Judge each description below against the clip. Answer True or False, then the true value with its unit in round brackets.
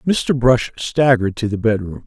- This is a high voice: False (120 Hz)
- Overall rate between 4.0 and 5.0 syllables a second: True (4.4 syllables/s)